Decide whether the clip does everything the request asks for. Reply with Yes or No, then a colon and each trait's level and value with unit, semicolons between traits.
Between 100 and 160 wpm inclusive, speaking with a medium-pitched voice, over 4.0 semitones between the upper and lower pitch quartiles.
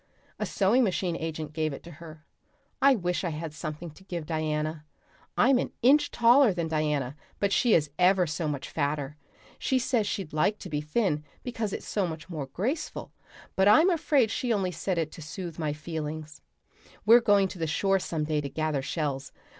No: average, 195 wpm; medium, 170 Hz; average, 5.0 semitones